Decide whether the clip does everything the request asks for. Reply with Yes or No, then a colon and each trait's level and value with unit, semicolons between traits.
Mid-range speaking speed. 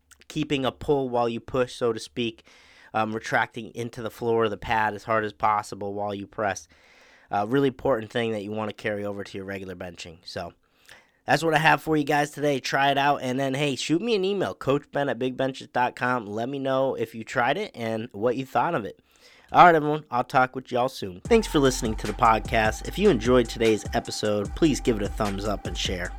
No: fast, 230 wpm